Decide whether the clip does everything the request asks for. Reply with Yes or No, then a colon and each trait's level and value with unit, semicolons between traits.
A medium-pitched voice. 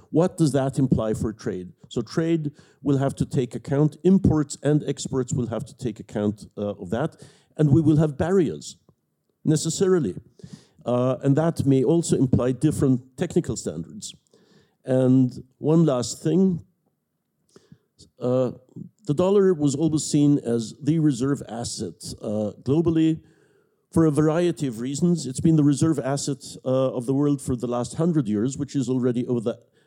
Yes: medium, 145 Hz